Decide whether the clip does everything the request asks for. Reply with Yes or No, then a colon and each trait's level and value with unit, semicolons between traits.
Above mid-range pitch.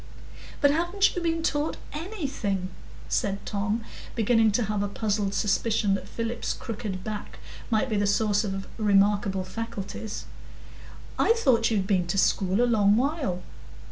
Yes: high, 215 Hz